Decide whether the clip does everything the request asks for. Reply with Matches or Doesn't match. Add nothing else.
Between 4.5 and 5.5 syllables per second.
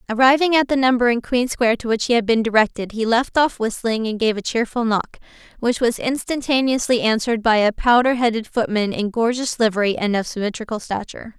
Doesn't match